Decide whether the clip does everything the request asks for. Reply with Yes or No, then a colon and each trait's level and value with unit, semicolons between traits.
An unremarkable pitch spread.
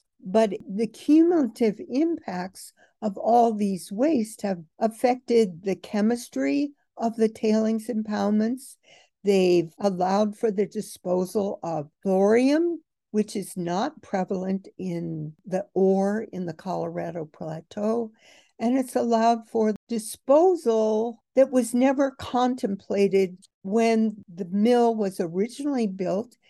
Yes: average, 3.6 semitones